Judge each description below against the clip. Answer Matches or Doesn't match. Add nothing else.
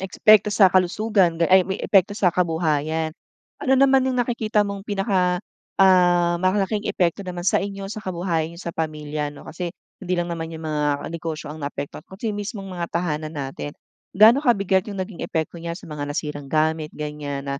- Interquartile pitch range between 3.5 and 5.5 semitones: Matches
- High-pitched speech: Doesn't match